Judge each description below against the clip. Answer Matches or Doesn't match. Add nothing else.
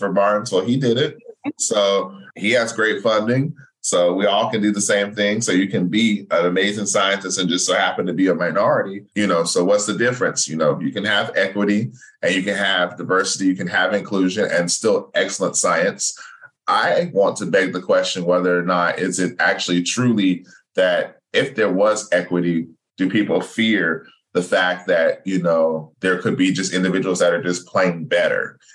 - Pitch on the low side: Matches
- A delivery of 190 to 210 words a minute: Matches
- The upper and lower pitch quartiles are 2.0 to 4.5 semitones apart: Matches